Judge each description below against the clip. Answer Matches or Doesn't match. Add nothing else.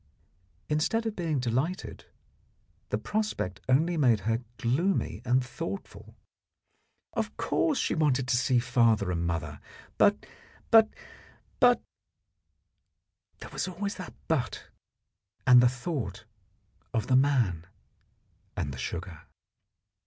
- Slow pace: Matches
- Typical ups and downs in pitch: Doesn't match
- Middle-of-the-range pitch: Doesn't match